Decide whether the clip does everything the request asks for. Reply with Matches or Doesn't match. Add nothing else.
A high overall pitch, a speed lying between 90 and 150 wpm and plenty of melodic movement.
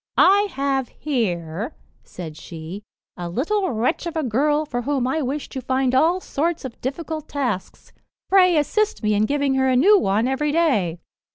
Doesn't match